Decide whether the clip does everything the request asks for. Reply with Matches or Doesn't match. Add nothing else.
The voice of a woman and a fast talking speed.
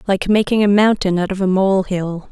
Matches